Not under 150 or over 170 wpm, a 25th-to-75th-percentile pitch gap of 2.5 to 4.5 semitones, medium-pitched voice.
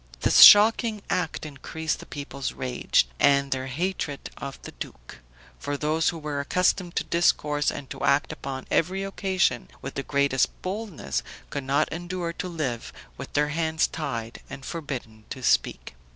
Yes: average, 160 wpm; average, 4.2 semitones; medium, 150 Hz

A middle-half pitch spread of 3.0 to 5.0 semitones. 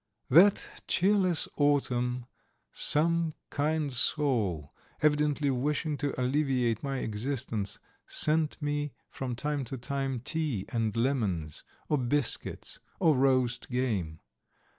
Yes: average, 3.6 semitones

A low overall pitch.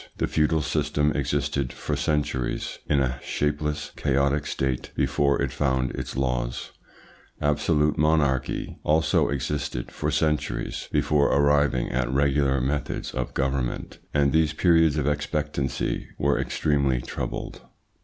Yes: very low, 70 Hz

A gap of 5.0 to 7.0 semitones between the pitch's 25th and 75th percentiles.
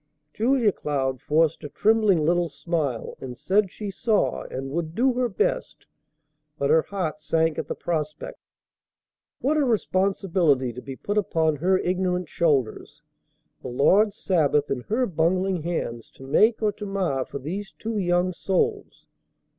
Yes: average, 5.3 semitones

